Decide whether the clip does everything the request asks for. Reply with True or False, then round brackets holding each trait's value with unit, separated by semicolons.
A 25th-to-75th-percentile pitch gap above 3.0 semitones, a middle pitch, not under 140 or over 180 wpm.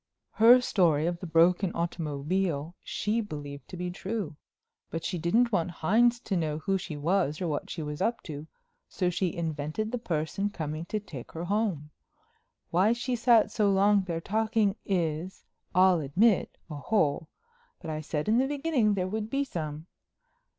True (5.2 semitones; 180 Hz; 165 wpm)